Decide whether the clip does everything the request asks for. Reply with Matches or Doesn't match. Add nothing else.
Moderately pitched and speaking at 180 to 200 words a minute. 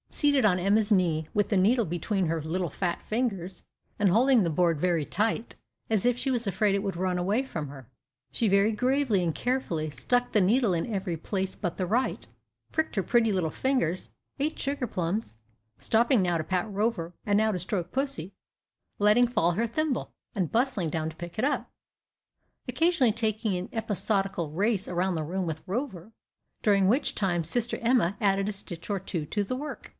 Doesn't match